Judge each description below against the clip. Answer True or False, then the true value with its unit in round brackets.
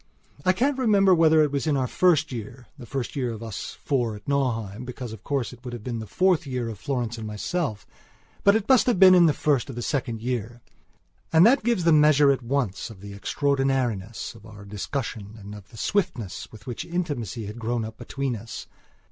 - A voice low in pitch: True (125 Hz)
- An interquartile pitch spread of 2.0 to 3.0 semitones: False (5.5 semitones)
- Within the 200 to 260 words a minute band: True (205 wpm)